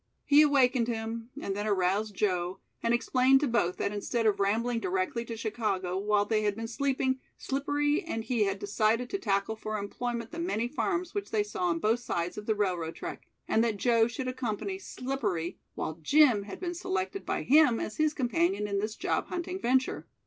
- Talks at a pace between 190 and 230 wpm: Yes, average, 195 wpm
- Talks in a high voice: Yes, high, 230 Hz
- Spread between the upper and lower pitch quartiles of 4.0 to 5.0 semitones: Yes, average, 4.6 semitones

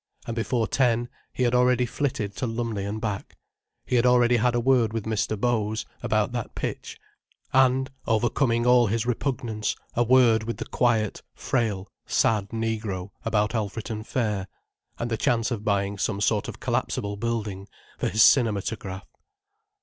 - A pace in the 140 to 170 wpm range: Yes, average, 155 wpm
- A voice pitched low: Yes, low, 115 Hz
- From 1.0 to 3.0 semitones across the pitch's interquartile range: Yes, narrow, 2.4 semitones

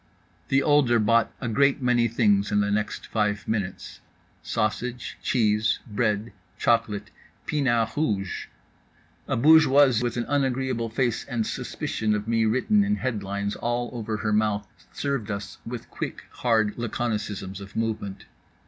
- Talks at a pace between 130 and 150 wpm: Yes, average, 140 wpm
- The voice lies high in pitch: No, low, 115 Hz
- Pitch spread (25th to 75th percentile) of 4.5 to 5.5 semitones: No, average, 2.9 semitones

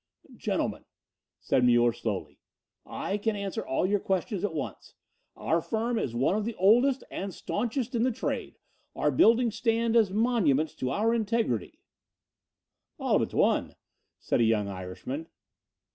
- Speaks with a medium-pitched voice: No, high, 205 Hz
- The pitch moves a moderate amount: No, wide, 8.6 semitones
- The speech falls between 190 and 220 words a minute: No, average, 150 wpm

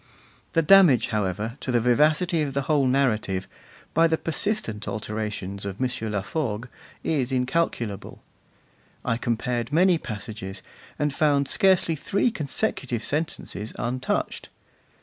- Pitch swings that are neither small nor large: No, wide, 6.1 semitones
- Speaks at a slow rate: Yes, slow, 120 wpm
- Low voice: Yes, low, 130 Hz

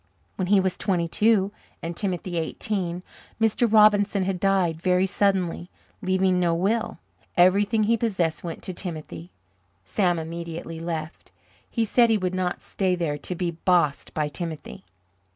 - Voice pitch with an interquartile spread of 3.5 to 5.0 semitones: No, average, 3.0 semitones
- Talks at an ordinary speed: Yes, average, 150 wpm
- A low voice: No, medium, 180 Hz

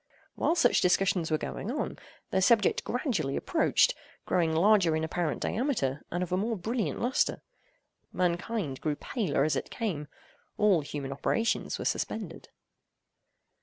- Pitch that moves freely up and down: Yes, wide, 6.1 semitones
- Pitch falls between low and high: Yes, medium, 180 Hz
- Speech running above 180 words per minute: No, average, 140 wpm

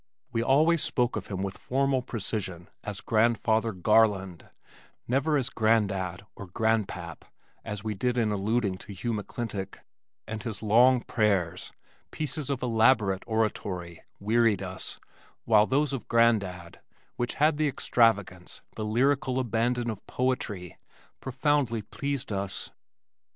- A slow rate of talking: Yes, slow, 130 wpm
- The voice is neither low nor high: No, low, 110 Hz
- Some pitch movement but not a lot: Yes, average, 4.1 semitones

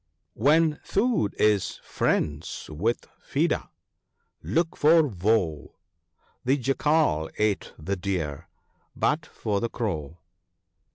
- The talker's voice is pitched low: Yes, low, 105 Hz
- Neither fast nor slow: No, slow, 100 wpm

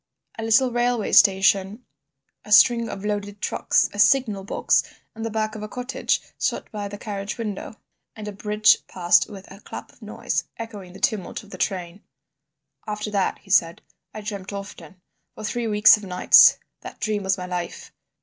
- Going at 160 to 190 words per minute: Yes, average, 180 wpm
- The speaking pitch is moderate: No, high, 210 Hz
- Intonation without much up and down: Yes, narrow, 2.0 semitones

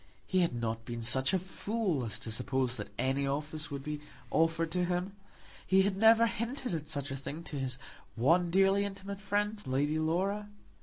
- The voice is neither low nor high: Yes, medium, 165 Hz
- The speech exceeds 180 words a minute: Yes, average, 190 wpm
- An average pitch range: No, wide, 6.1 semitones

